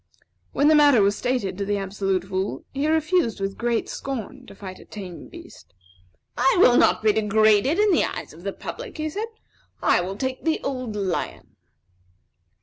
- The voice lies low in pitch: No, high, 220 Hz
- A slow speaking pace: No, average, 180 wpm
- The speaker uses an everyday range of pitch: No, wide, 6.4 semitones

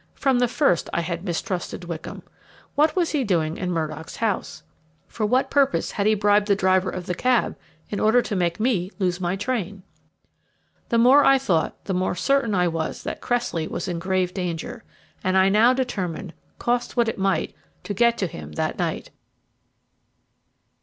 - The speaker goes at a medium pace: Yes, average, 180 wpm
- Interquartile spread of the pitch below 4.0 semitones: No, average, 5.1 semitones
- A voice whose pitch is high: Yes, high, 195 Hz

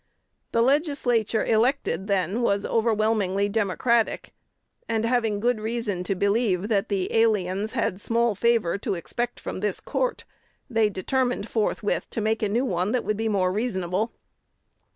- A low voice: No, high, 220 Hz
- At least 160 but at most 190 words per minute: No, average, 150 wpm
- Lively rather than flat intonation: No, average, 2.9 semitones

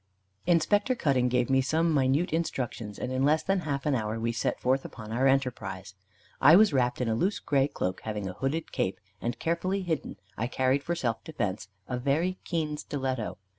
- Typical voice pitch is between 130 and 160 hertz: Yes, low, 135 Hz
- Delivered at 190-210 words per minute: Yes, average, 195 wpm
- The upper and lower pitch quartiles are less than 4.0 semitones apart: No, average, 5.1 semitones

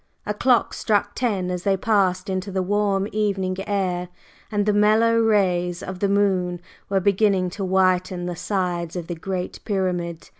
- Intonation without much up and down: Yes, narrow, 2.3 semitones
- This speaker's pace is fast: No, average, 165 wpm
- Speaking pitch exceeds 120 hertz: Yes, high, 190 Hz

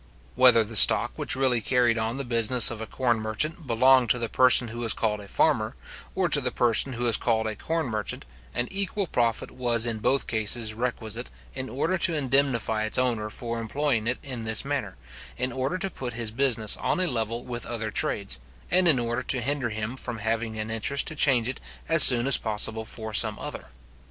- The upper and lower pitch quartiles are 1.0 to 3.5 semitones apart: Yes, average, 2.8 semitones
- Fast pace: Yes, fast, 210 wpm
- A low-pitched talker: Yes, low, 120 Hz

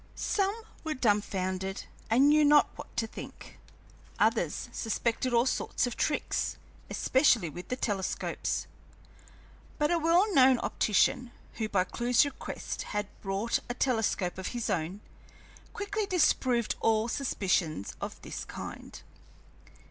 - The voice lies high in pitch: Yes, high, 235 Hz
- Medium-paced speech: No, slow, 125 wpm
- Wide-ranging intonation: Yes, wide, 6.3 semitones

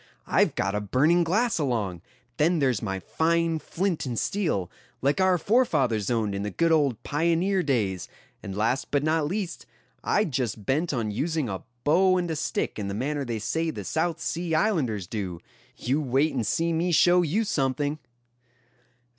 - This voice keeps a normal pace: Yes, average, 175 wpm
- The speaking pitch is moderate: Yes, medium, 150 Hz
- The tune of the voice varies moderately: No, wide, 6.8 semitones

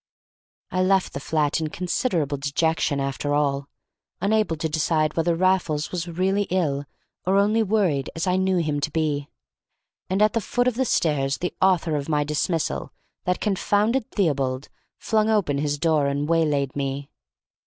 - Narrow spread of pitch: No, average, 4.6 semitones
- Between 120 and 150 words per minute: No, average, 160 wpm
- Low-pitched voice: No, medium, 160 Hz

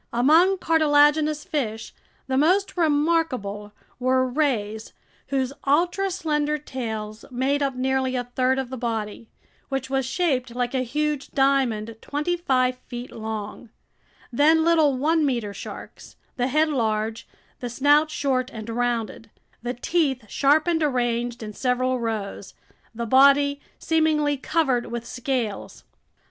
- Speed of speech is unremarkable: No, slow, 130 wpm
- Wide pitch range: No, average, 3.9 semitones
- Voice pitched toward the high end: Yes, very high, 260 Hz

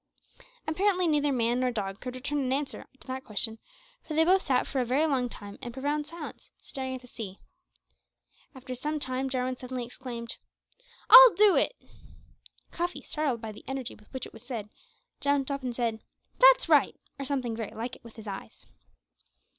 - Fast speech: No, average, 185 wpm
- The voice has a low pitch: No, very high, 260 Hz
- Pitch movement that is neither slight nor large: Yes, average, 3.8 semitones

